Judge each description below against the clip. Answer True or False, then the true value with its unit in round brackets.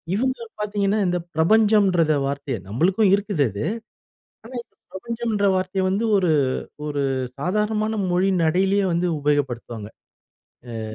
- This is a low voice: False (190 Hz)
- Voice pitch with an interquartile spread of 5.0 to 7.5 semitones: True (5.3 semitones)